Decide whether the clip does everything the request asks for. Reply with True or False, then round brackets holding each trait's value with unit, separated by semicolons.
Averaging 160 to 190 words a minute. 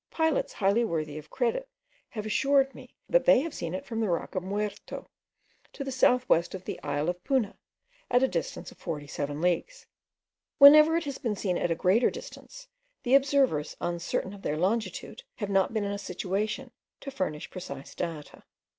True (185 wpm)